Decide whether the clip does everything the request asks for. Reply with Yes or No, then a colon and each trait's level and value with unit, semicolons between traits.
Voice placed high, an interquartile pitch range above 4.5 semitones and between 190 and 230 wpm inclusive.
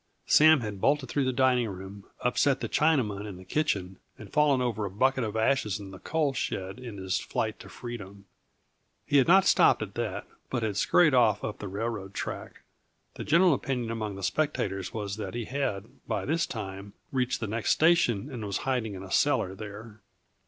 No: low, 115 Hz; average, 5.1 semitones; average, 195 wpm